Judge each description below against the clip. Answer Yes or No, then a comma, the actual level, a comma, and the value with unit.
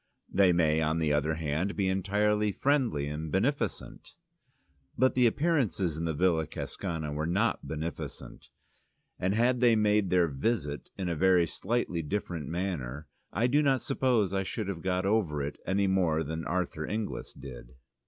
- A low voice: Yes, very low, 90 Hz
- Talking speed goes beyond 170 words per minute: No, average, 165 wpm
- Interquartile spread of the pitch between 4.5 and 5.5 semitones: Yes, average, 5.1 semitones